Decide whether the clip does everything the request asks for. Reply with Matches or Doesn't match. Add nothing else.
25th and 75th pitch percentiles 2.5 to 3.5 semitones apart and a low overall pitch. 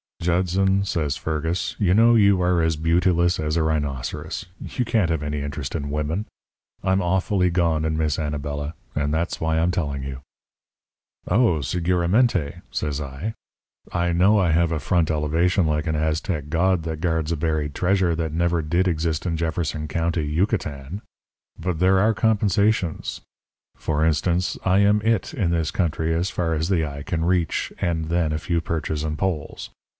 Matches